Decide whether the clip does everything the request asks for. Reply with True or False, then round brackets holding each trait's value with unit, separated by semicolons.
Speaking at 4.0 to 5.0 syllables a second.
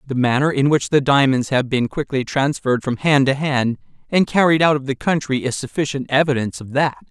False (5.6 syllables/s)